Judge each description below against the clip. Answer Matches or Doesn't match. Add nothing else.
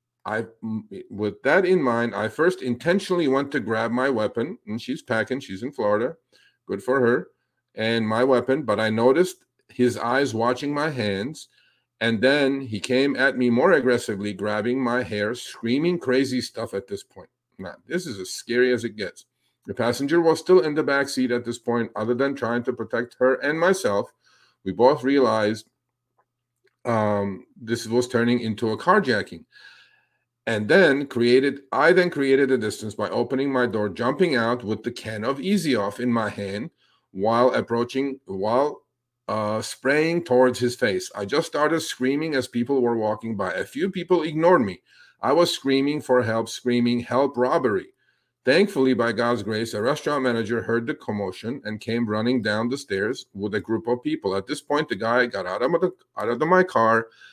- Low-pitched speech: Matches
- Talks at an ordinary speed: Matches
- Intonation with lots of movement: Doesn't match